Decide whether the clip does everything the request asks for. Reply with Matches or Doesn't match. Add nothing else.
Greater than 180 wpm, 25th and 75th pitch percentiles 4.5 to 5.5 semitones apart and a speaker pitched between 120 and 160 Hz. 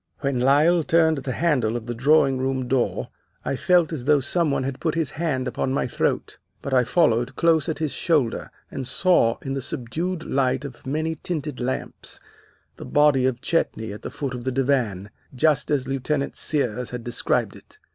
Doesn't match